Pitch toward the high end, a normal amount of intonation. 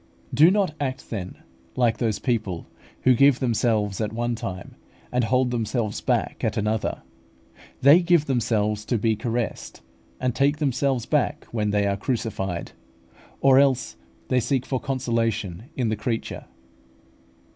No: low, 120 Hz; average, 3.6 semitones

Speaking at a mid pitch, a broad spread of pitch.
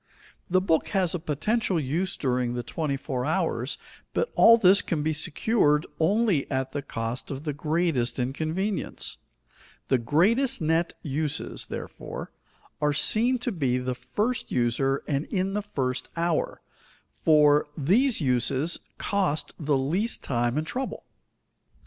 Yes: medium, 155 Hz; wide, 6.0 semitones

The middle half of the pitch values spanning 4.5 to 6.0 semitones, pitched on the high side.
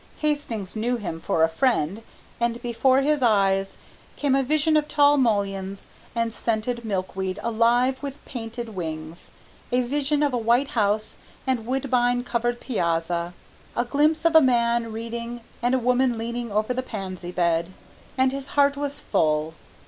Yes: average, 4.8 semitones; high, 235 Hz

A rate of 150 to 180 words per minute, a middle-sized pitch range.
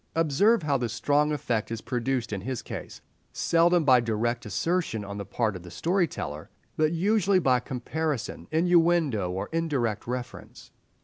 No: average, 160 wpm; wide, 6.3 semitones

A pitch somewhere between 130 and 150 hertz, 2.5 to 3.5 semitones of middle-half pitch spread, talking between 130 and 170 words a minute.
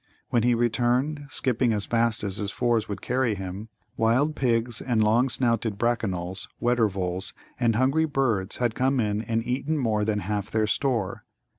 No: low, 115 Hz; average, 3.1 semitones; average, 165 wpm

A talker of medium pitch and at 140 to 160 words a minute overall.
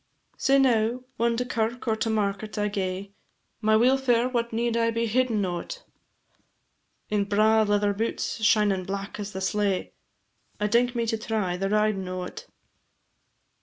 No: high, 215 Hz; average, 155 wpm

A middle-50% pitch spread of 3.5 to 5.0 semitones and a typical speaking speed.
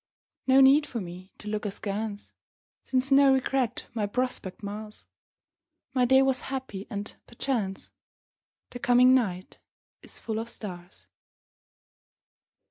No: average, 4.4 semitones; slow, 125 wpm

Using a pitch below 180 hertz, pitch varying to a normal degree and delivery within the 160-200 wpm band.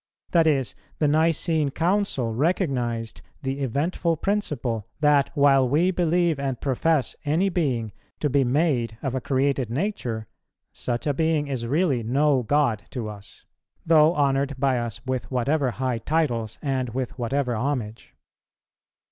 No: low, 135 Hz; average, 4.3 semitones; average, 140 wpm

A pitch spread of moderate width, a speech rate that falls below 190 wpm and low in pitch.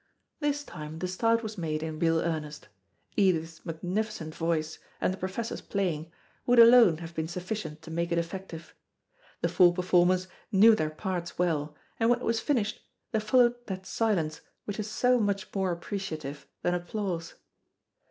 No: average, 4.6 semitones; average, 160 wpm; medium, 180 Hz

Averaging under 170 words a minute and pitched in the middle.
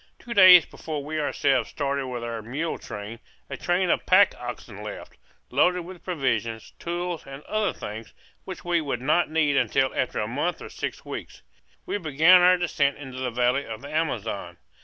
No: average, 180 wpm; medium, 145 Hz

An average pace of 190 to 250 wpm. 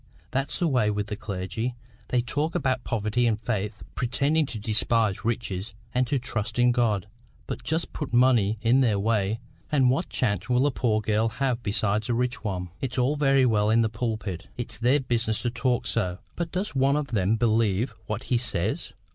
Yes: average, 195 wpm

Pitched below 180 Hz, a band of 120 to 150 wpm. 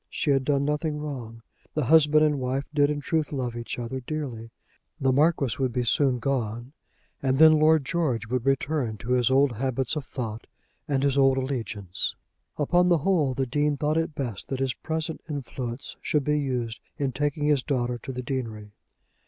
No: low, 135 Hz; average, 185 wpm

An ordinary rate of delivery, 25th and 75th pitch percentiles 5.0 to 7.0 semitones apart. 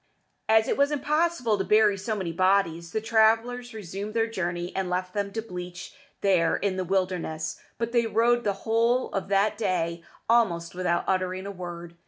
No: average, 180 wpm; average, 3.9 semitones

